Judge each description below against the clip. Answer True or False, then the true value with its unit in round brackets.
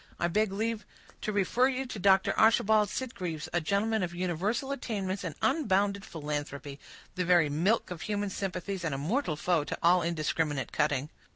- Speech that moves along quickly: False (170 wpm)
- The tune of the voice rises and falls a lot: False (4.7 semitones)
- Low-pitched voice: False (185 Hz)